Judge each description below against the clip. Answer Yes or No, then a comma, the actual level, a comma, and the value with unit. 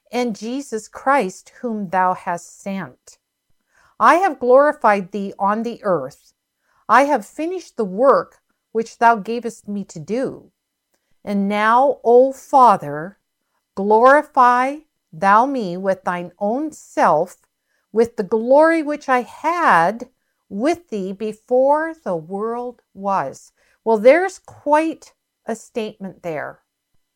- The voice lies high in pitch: Yes, high, 230 Hz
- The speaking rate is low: Yes, slow, 120 wpm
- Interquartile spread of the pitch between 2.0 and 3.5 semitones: No, average, 5.1 semitones